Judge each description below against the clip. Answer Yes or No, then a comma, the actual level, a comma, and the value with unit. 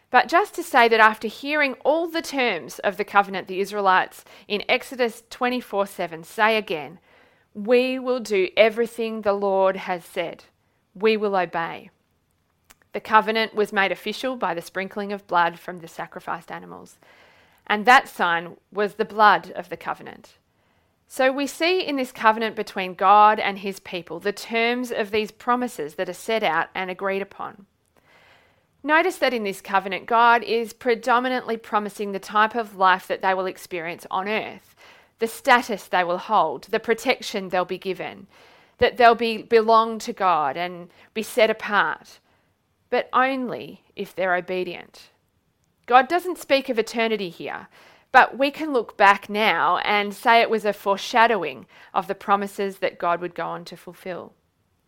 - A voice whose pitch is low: No, high, 210 Hz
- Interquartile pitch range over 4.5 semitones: No, average, 3.9 semitones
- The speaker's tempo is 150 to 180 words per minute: Yes, average, 165 wpm